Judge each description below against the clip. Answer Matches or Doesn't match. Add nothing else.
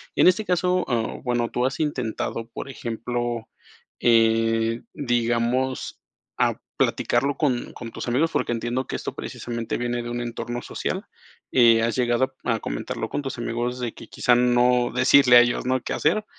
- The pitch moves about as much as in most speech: Doesn't match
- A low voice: Matches